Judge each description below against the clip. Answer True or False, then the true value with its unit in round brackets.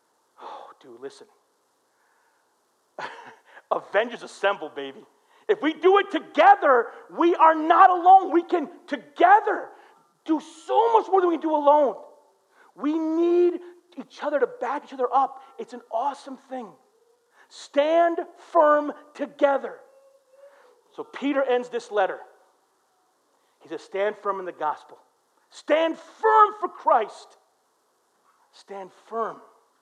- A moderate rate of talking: False (115 wpm)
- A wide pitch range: True (7.7 semitones)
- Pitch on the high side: True (330 Hz)